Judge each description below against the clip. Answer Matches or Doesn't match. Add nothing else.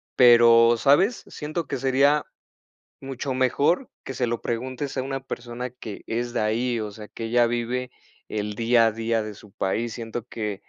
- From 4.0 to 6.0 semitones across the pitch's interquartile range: Doesn't match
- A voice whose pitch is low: Matches